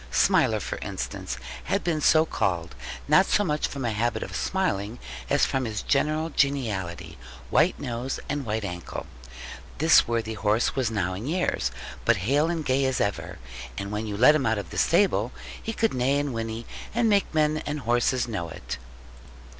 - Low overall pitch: Yes, low, 125 Hz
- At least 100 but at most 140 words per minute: No, average, 180 wpm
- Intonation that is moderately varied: No, wide, 6.0 semitones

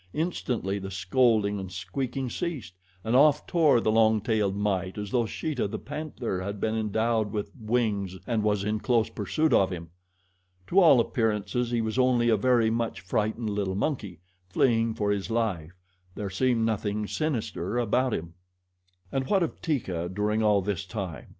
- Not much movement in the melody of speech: No, average, 3.6 semitones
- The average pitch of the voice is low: Yes, low, 110 Hz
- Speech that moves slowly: No, average, 170 wpm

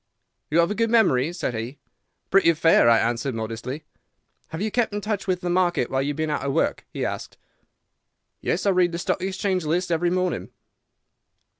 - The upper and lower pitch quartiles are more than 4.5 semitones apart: Yes, wide, 5.4 semitones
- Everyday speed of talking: Yes, average, 195 wpm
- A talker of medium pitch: Yes, medium, 175 Hz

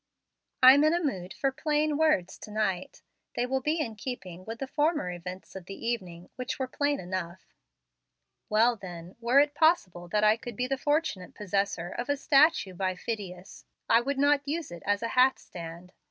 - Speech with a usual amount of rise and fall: No, wide, 7.3 semitones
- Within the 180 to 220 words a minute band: Yes, average, 190 wpm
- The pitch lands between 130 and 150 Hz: No, high, 230 Hz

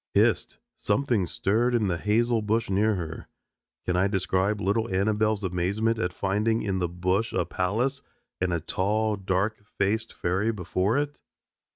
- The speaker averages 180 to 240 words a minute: No, average, 160 wpm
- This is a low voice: Yes, low, 105 Hz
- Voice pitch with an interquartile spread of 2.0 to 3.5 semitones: Yes, average, 3.1 semitones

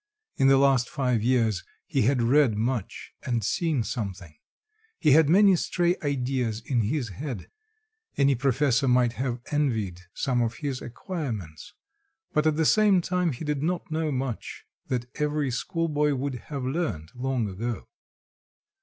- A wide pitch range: No, average, 4.1 semitones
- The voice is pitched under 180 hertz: Yes, low, 135 Hz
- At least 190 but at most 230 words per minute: No, average, 150 wpm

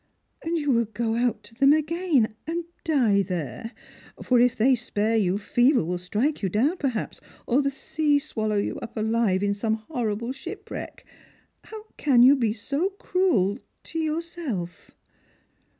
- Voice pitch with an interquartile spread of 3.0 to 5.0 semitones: No, wide, 5.4 semitones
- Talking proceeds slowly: No, average, 165 wpm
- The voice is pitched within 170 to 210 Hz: No, high, 240 Hz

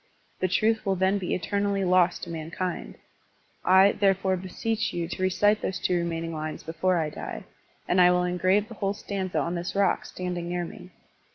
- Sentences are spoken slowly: No, average, 185 wpm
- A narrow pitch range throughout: Yes, narrow, 2.1 semitones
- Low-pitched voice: No, medium, 185 Hz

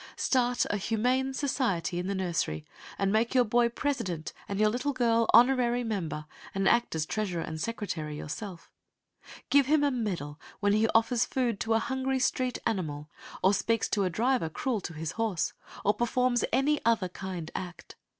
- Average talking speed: Yes, average, 175 wpm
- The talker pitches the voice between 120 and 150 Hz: No, high, 225 Hz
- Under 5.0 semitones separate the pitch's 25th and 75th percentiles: No, average, 5.3 semitones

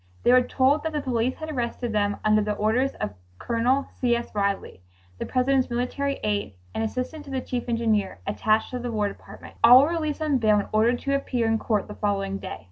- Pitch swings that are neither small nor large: Yes, average, 3.7 semitones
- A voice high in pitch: Yes, high, 235 Hz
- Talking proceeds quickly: Yes, fast, 215 wpm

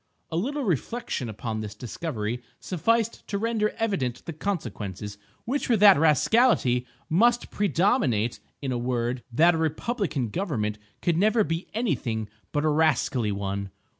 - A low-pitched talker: No, medium, 155 Hz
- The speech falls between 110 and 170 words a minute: Yes, average, 140 wpm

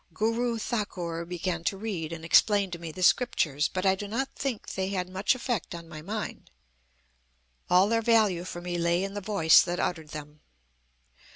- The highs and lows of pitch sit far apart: No, average, 4.0 semitones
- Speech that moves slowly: No, average, 185 wpm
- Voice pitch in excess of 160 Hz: Yes, medium, 185 Hz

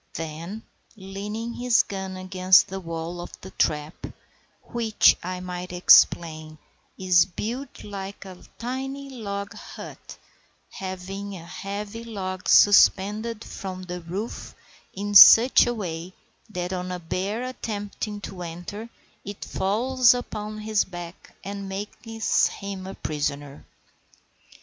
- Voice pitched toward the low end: No, high, 195 Hz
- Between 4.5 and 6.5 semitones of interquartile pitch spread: No, average, 3.0 semitones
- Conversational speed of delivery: No, slow, 120 wpm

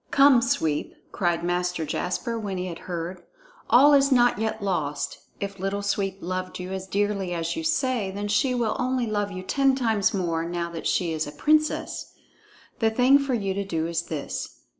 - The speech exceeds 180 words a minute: Yes, average, 190 wpm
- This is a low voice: No, high, 195 Hz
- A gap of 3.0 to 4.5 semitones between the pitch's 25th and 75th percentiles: No, wide, 5.4 semitones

